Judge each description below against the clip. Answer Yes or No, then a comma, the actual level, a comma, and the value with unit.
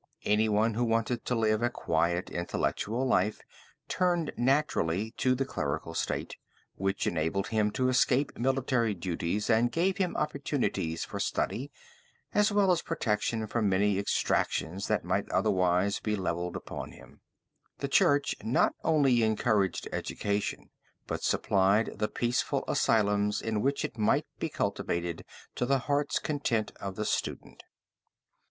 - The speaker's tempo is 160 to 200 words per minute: No, average, 140 wpm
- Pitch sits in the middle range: No, low, 110 Hz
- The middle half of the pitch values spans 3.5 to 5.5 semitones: Yes, average, 5.1 semitones